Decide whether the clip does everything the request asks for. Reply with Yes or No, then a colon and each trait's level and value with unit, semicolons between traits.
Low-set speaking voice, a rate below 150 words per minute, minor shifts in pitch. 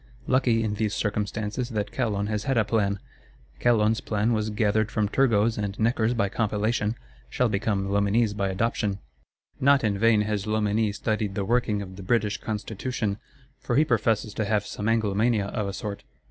No: low, 105 Hz; average, 175 wpm; narrow, 2.0 semitones